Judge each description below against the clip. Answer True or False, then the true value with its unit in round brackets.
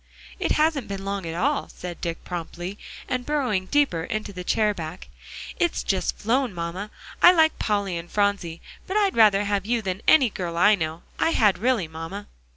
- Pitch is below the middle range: False (200 Hz)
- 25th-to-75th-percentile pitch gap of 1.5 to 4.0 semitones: False (5.6 semitones)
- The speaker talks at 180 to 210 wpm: True (185 wpm)